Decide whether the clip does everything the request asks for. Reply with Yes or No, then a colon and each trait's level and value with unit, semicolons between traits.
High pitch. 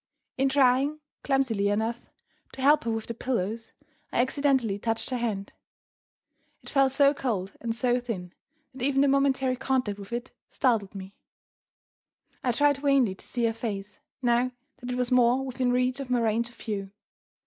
Yes: high, 245 Hz